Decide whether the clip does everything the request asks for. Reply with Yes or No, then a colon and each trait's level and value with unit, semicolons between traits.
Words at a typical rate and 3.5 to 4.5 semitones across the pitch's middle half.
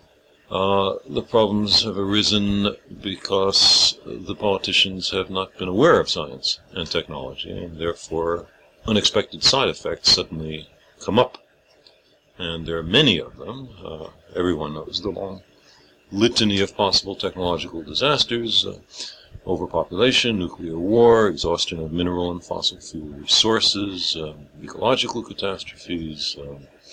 No: slow, 125 wpm; average, 3.8 semitones